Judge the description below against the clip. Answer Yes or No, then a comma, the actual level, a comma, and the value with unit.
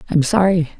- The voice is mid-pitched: Yes, medium, 175 Hz